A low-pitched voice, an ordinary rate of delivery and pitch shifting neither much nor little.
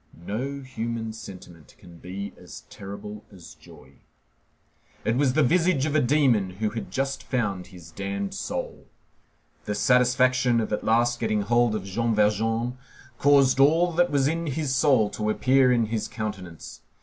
Yes: low, 115 Hz; average, 160 wpm; average, 4.5 semitones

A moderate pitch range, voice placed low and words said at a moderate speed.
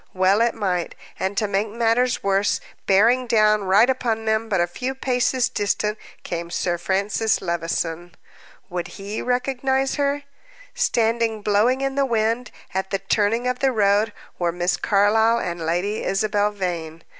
No: average, 3.8 semitones; high, 210 Hz; average, 155 wpm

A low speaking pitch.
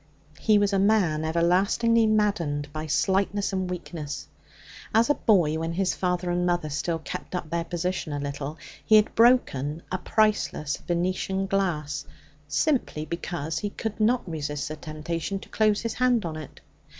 No: medium, 175 Hz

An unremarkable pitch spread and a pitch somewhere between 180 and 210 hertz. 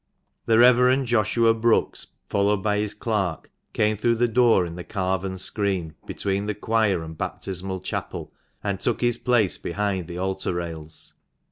No: average, 3.4 semitones; low, 100 Hz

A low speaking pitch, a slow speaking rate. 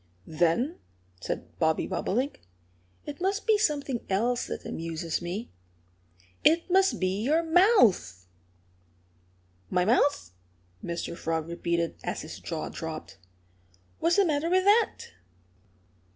No: high, 245 Hz; slow, 115 wpm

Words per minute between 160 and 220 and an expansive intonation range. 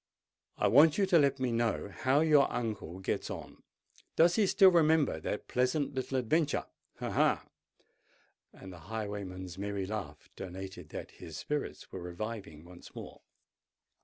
No: average, 140 wpm; wide, 7.6 semitones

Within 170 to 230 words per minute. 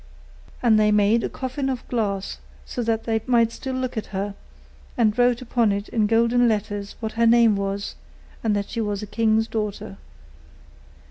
Yes: average, 180 wpm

